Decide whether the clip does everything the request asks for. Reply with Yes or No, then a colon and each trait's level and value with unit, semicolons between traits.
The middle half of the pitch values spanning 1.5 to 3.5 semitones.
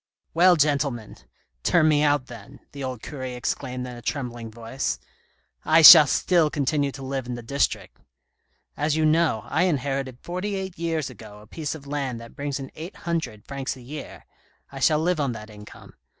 No: average, 4.1 semitones